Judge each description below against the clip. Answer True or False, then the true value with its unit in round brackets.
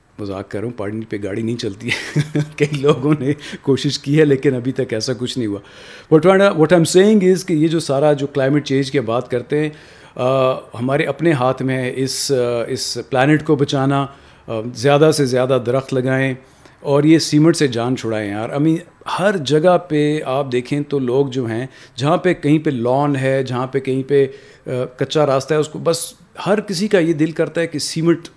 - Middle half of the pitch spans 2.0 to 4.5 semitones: True (3.3 semitones)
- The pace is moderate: False (205 wpm)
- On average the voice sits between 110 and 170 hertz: True (140 Hz)